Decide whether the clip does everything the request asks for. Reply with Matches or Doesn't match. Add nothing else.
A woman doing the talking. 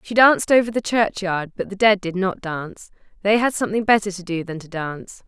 Matches